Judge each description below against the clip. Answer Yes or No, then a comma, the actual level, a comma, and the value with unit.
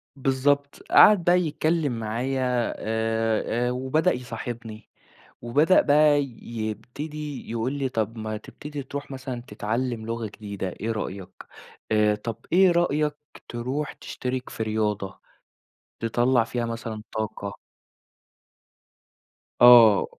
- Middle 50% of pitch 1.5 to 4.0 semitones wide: No, average, 4.4 semitones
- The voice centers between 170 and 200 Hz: No, low, 120 Hz